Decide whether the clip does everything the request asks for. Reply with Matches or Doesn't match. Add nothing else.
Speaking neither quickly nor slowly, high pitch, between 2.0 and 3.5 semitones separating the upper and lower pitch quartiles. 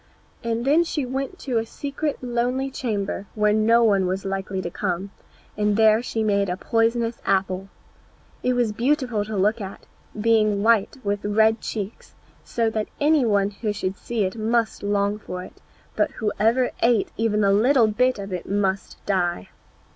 Matches